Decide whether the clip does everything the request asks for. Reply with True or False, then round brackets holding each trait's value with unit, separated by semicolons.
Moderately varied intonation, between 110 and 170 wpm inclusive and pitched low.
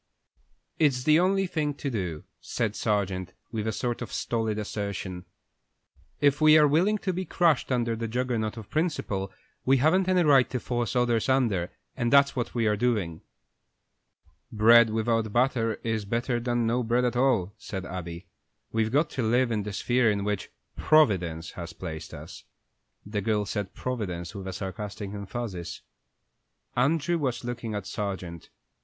True (4.2 semitones; 160 wpm; 115 Hz)